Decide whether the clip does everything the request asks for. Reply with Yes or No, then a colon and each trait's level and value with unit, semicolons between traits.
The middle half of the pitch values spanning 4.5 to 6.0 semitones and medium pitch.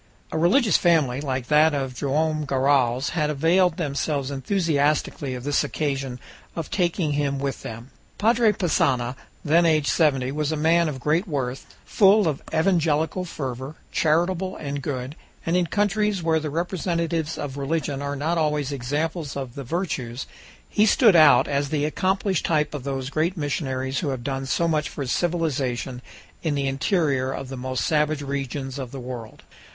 No: average, 3.6 semitones; medium, 150 Hz